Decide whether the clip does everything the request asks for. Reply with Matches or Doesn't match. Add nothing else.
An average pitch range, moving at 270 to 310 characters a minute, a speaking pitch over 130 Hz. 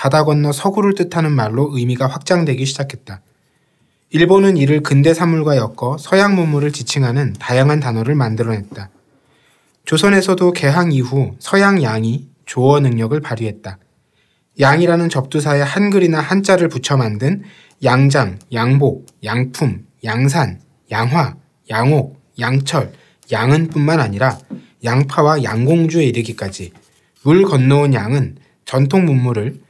Matches